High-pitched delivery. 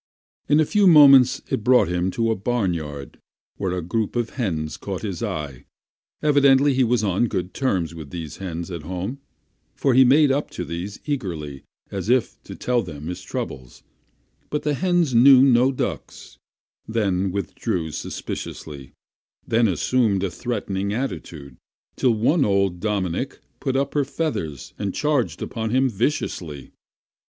No: low, 105 Hz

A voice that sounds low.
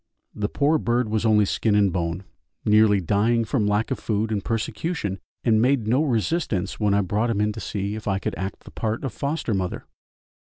Yes: low, 110 Hz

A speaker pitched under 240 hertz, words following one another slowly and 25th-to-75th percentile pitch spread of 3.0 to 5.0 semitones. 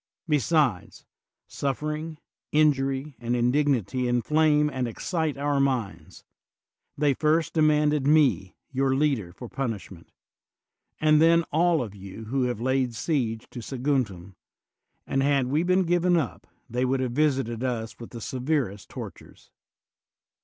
Yes: low, 135 Hz; slow, 130 wpm; average, 4.0 semitones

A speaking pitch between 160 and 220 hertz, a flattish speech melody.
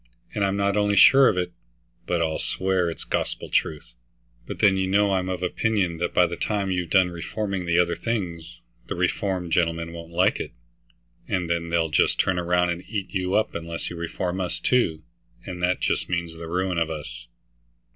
No: very low, 90 Hz; narrow, 2.3 semitones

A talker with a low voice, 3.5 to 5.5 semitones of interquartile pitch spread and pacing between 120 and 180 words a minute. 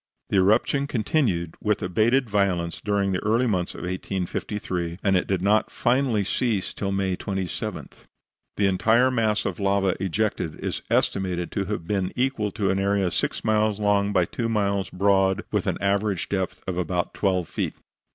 No: low, 100 Hz; narrow, 2.5 semitones; average, 170 wpm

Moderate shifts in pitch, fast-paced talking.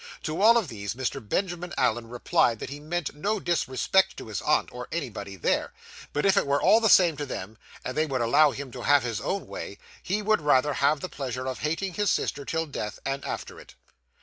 No: wide, 5.9 semitones; fast, 225 wpm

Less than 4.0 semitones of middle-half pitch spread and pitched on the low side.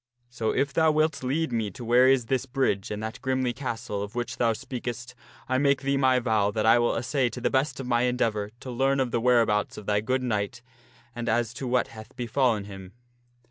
Yes: average, 2.8 semitones; low, 120 Hz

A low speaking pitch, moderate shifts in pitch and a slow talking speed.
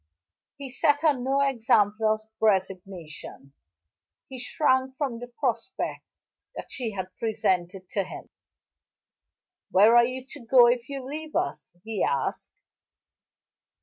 No: high, 240 Hz; average, 4.5 semitones; slow, 120 wpm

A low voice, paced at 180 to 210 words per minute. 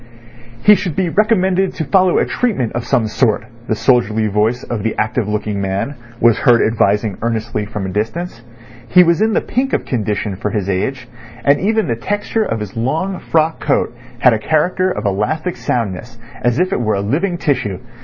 Yes: low, 120 Hz; average, 195 wpm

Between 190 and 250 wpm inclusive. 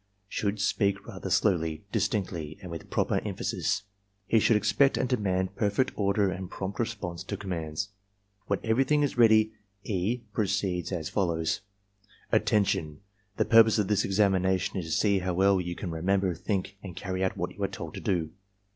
No: average, 175 wpm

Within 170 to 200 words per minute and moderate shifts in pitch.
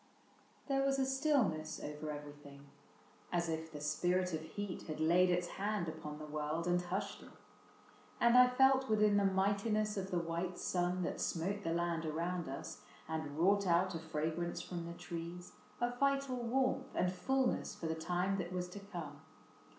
Yes: average, 175 wpm; average, 4.2 semitones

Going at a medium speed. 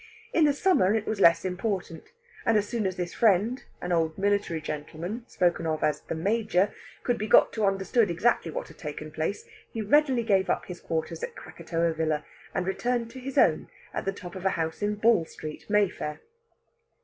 Yes: average, 195 wpm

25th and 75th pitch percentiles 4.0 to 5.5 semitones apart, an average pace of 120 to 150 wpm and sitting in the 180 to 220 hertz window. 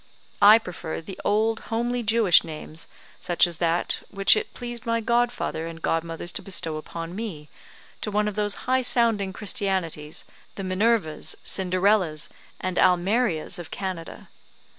Yes: average, 5.0 semitones; average, 140 wpm; high, 190 Hz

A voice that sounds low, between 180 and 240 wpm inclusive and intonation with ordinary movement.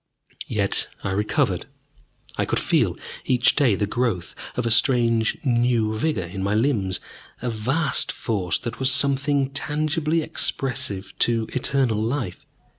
No: low, 120 Hz; slow, 135 wpm; average, 4.3 semitones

